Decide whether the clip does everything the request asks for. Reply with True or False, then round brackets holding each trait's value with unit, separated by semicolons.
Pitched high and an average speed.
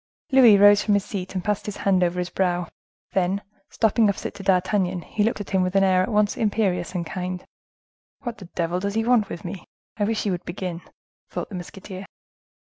False (195 Hz; 210 wpm)